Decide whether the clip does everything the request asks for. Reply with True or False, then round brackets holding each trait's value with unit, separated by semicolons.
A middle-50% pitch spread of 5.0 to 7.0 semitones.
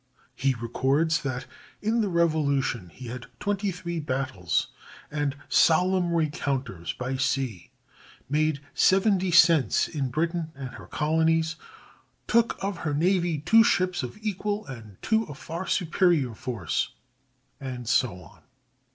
True (5.4 semitones)